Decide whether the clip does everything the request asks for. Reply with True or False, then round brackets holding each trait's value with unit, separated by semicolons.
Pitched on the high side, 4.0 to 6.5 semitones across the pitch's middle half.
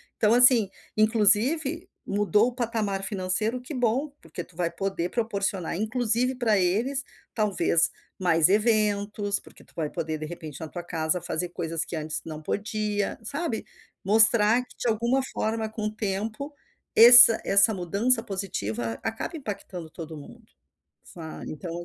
True (210 Hz; 4.6 semitones)